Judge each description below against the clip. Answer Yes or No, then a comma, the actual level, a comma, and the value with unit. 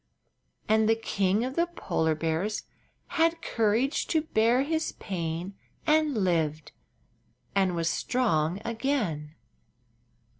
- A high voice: Yes, high, 215 Hz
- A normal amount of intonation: No, wide, 8.1 semitones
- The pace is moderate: No, slow, 110 wpm